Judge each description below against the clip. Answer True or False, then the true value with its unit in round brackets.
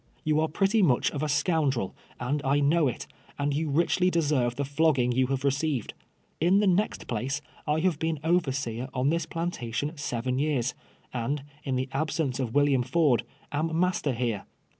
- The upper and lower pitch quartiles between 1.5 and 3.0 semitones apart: False (3.9 semitones)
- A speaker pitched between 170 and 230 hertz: False (145 Hz)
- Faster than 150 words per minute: True (175 wpm)